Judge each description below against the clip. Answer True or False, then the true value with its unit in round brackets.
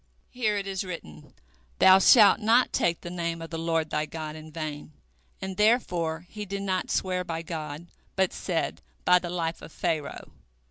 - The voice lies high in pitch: False (170 Hz)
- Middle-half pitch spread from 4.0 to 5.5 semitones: False (2.9 semitones)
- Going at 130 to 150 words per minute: False (180 wpm)